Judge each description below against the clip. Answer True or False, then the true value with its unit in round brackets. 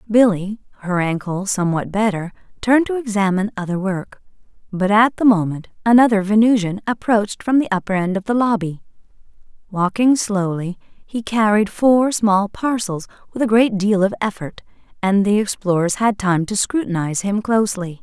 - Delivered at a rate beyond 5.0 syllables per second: True (5.2 syllables/s)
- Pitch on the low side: False (205 Hz)